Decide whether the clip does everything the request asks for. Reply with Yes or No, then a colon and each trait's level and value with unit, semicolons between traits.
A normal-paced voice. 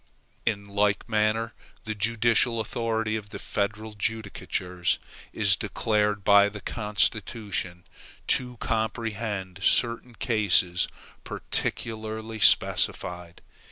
No: slow, 90 wpm